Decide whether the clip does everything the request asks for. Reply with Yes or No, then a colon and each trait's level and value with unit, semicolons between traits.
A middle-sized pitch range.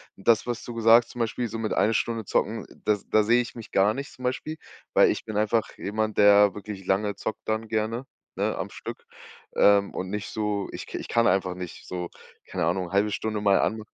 No: narrow, 2.3 semitones